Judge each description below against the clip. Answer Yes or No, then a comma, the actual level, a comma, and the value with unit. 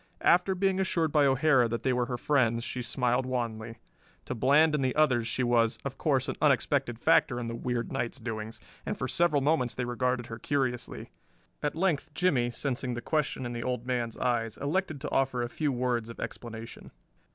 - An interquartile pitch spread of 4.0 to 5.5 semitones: No, average, 3.3 semitones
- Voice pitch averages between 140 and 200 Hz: No, low, 125 Hz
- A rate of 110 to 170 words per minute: No, average, 195 wpm